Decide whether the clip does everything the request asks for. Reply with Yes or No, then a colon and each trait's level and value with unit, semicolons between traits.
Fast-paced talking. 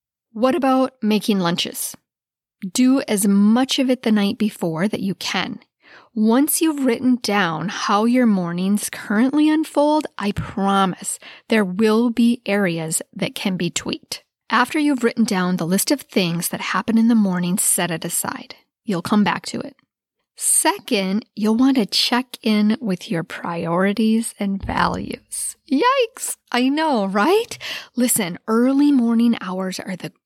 No: average, 150 wpm